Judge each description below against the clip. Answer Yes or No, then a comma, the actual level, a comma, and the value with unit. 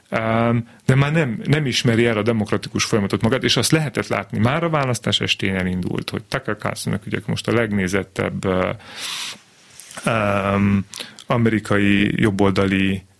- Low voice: Yes, low, 110 Hz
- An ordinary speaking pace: Yes, average, 135 wpm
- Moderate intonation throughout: Yes, average, 3.2 semitones